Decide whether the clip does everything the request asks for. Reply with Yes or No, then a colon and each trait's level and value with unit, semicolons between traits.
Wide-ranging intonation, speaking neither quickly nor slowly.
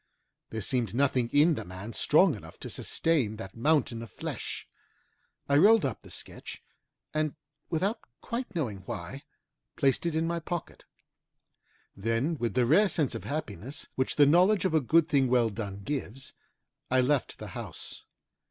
Yes: wide, 5.8 semitones; average, 160 wpm